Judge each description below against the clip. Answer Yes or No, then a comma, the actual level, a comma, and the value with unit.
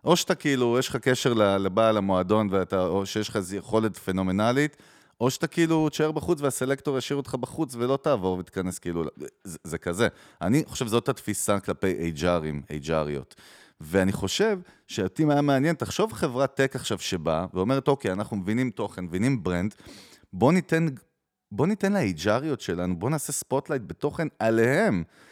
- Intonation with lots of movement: Yes, wide, 7.1 semitones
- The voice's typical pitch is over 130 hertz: No, low, 120 Hz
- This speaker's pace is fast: Yes, fast, 160 wpm